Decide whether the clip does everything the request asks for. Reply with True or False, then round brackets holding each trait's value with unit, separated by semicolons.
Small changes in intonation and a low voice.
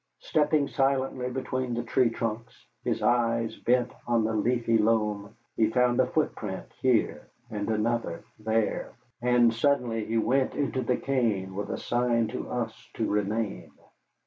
True (2.2 semitones; 115 Hz)